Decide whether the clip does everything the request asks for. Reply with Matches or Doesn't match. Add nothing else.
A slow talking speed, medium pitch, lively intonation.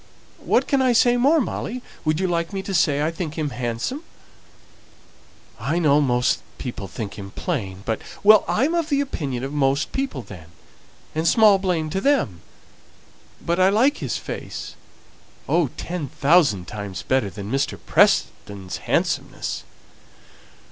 Doesn't match